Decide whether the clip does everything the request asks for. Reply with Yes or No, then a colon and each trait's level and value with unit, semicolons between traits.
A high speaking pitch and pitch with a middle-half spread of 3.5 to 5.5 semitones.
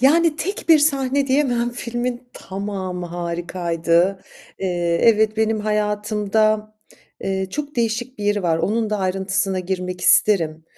Yes: high, 210 Hz; average, 4.5 semitones